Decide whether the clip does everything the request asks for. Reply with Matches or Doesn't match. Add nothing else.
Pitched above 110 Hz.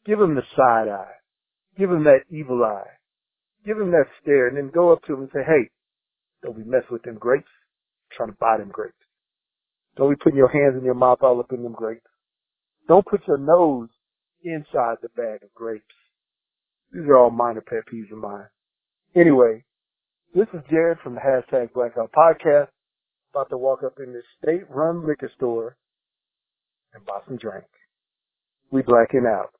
Matches